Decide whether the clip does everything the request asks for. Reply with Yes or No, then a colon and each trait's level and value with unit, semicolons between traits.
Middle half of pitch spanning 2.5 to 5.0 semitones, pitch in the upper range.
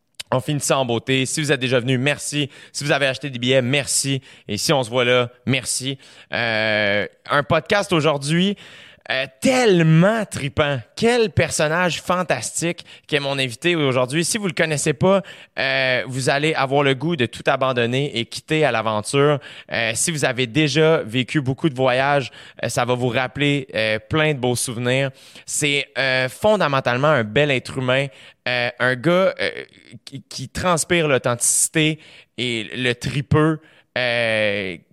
No: average, 3.8 semitones; low, 135 Hz